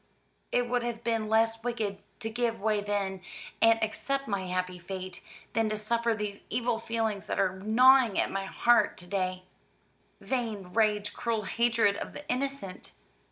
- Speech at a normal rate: Yes, average, 160 wpm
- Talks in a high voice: Yes, high, 220 Hz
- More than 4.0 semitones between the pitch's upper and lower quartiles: No, average, 3.0 semitones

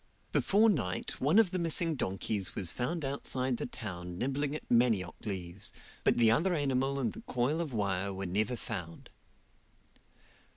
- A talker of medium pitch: No, low, 125 Hz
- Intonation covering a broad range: Yes, wide, 7.0 semitones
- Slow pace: No, average, 160 wpm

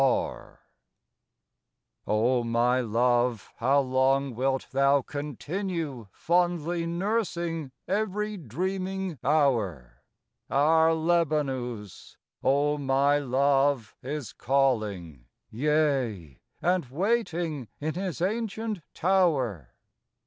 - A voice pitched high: No, medium, 140 Hz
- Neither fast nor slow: No, slow, 85 wpm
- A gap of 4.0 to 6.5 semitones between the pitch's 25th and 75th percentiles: Yes, wide, 5.6 semitones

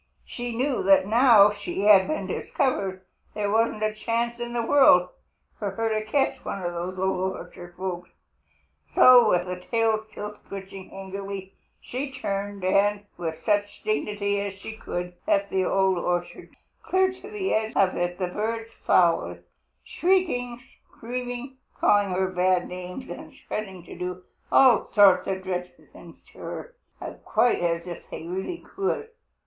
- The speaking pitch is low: No, high, 200 Hz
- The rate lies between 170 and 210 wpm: No, average, 155 wpm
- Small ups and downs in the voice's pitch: No, average, 4.1 semitones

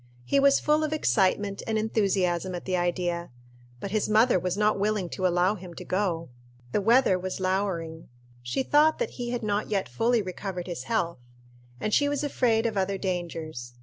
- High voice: Yes, high, 195 Hz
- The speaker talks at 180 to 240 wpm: Yes, average, 185 wpm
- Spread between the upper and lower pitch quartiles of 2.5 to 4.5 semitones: Yes, average, 4.0 semitones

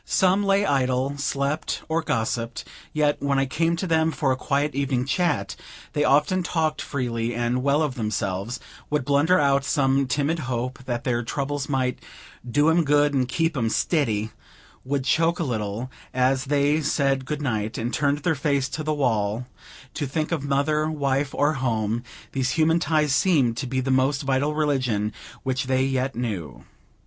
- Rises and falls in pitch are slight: No, average, 3.0 semitones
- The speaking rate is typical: Yes, average, 175 wpm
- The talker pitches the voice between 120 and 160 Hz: Yes, medium, 140 Hz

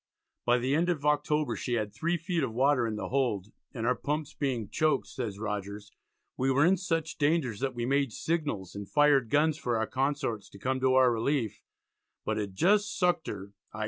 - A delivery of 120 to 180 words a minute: No, fast, 205 wpm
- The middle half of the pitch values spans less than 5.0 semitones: No, average, 5.3 semitones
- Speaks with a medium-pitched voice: No, low, 130 Hz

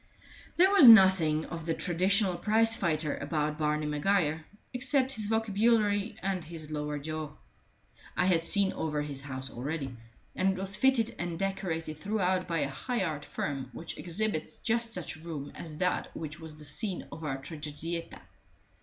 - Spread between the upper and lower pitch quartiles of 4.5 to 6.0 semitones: Yes, average, 5.0 semitones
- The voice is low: No, medium, 170 Hz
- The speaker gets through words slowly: No, average, 165 wpm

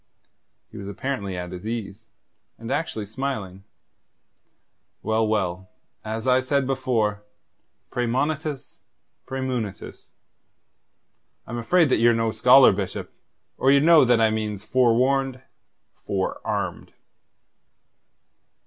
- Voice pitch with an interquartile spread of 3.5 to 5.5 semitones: Yes, average, 4.0 semitones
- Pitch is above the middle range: No, low, 115 Hz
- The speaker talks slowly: Yes, slow, 105 wpm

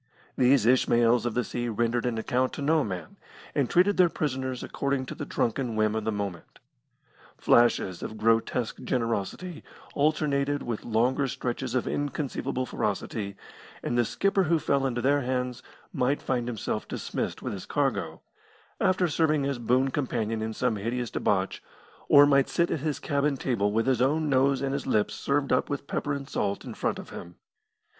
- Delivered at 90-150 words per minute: No, average, 175 wpm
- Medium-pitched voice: No, low, 130 Hz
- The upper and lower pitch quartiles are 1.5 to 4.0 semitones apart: Yes, average, 3.6 semitones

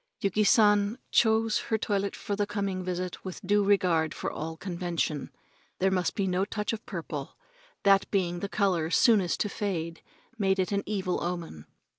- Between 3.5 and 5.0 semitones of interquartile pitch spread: No, average, 2.7 semitones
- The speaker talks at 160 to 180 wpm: Yes, average, 170 wpm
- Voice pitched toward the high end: Yes, high, 195 Hz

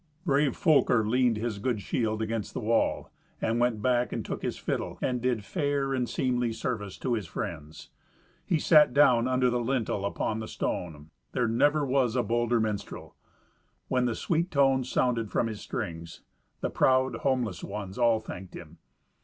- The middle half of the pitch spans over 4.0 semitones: No, average, 3.0 semitones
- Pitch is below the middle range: Yes, low, 120 Hz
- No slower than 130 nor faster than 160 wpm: No, average, 170 wpm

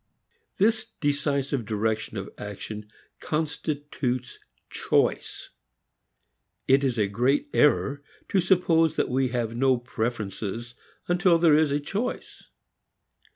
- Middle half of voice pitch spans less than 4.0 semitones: No, average, 5.3 semitones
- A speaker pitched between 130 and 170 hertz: Yes, low, 135 Hz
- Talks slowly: Yes, slow, 110 wpm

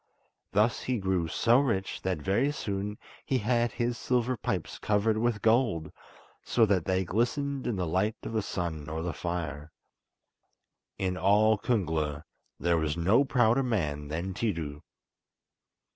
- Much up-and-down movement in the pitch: Yes, wide, 5.9 semitones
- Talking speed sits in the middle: Yes, average, 145 wpm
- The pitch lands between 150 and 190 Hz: No, low, 100 Hz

